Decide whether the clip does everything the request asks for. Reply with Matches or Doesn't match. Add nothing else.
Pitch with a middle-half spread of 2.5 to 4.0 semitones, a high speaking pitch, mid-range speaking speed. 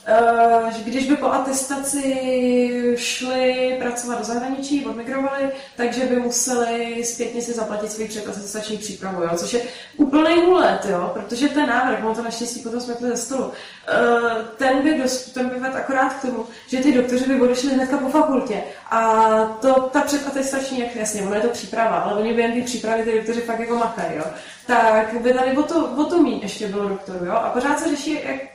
Doesn't match